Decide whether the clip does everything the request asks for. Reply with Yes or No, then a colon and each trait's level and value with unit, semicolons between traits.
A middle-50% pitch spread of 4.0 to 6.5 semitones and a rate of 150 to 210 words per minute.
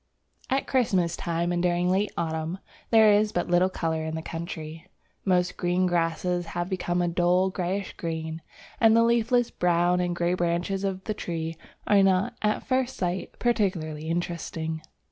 No: narrow, 2.4 semitones; average, 165 wpm